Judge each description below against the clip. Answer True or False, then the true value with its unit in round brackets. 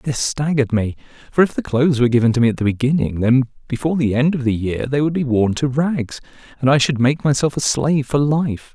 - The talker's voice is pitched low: True (130 Hz)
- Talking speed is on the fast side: True (245 wpm)